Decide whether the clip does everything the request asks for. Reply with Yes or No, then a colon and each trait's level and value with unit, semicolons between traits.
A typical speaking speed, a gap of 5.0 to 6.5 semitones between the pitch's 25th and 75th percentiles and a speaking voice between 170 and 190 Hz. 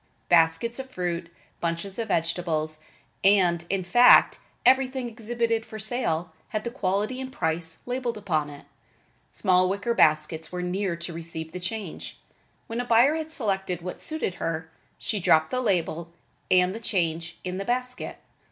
Yes: average, 160 wpm; wide, 5.6 semitones; medium, 185 Hz